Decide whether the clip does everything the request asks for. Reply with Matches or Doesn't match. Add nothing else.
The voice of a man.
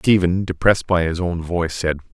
Matches